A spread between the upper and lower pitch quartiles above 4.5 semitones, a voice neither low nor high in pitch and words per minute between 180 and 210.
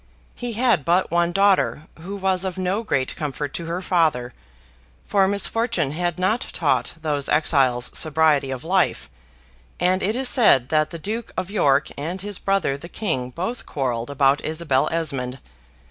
No: wide, 5.4 semitones; medium, 170 Hz; average, 160 wpm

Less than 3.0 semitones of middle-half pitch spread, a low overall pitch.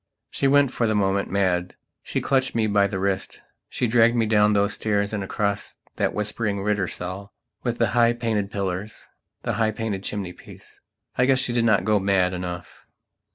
Yes: narrow, 2.6 semitones; low, 105 Hz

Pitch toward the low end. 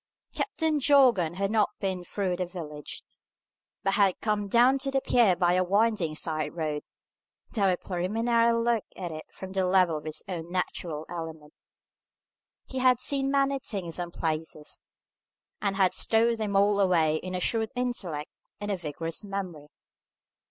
No: high, 190 Hz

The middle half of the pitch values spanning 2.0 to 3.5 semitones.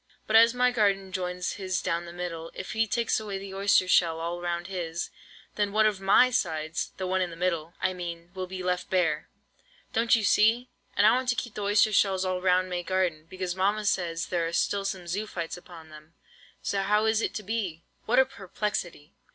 Yes: average, 3.2 semitones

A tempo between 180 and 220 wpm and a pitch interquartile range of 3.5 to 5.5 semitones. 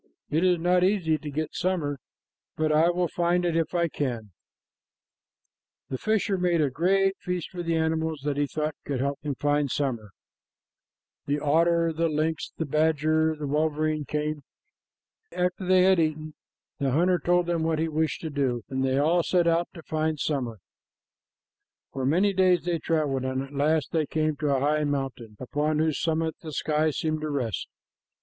No: average, 185 wpm; average, 2.7 semitones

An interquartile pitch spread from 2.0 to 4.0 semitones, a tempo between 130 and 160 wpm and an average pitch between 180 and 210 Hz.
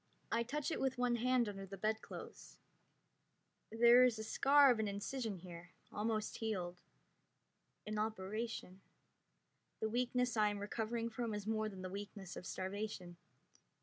No: average, 3.0 semitones; average, 150 wpm; high, 220 Hz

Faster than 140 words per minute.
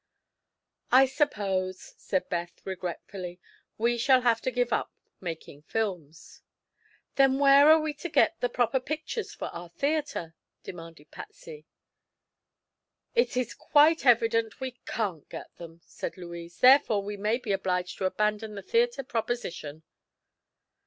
No: slow, 135 wpm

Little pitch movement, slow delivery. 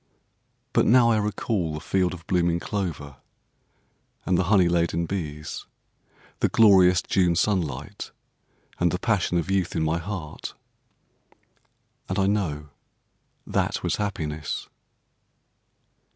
No: average, 3.6 semitones; slow, 120 wpm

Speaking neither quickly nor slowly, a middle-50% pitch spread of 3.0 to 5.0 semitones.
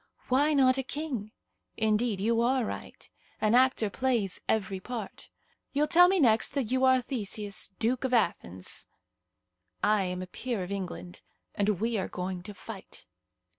Yes: average, 160 wpm; average, 4.6 semitones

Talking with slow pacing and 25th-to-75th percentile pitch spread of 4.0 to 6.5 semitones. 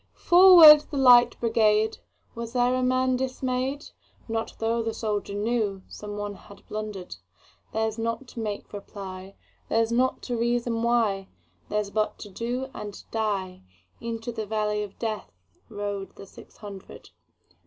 No: slow, 120 wpm; average, 3.0 semitones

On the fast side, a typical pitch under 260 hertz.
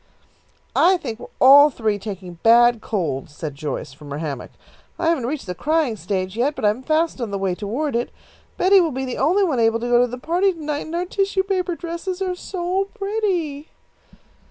No: fast, 210 wpm; very high, 265 Hz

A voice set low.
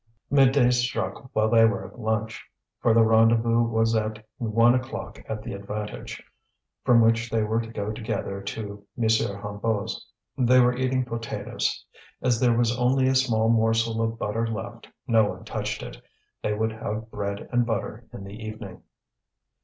Yes: low, 115 Hz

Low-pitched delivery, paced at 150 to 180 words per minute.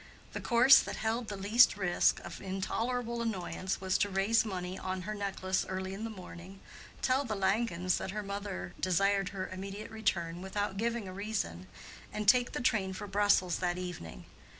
No: high, 195 Hz; average, 175 wpm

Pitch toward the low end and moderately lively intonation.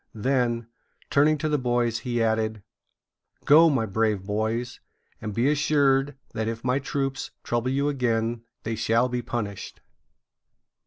Yes: low, 120 Hz; average, 3.2 semitones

